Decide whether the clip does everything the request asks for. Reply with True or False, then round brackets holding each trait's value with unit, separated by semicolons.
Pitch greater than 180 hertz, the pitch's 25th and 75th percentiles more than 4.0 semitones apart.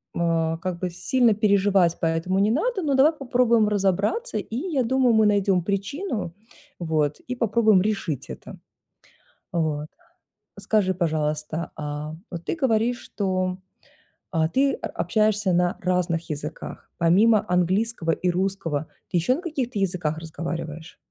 True (190 Hz; 5.2 semitones)